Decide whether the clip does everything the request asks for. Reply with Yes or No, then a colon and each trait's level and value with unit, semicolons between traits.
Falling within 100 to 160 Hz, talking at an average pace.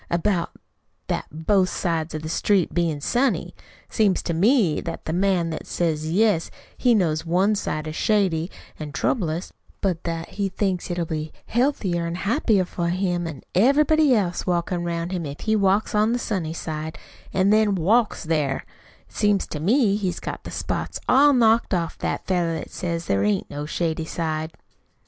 No: medium, 175 Hz; average, 175 wpm